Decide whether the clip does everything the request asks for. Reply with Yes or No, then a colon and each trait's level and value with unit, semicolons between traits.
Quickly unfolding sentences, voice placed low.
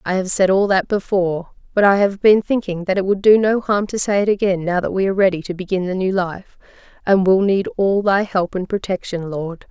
No: fast, 245 wpm; high, 190 Hz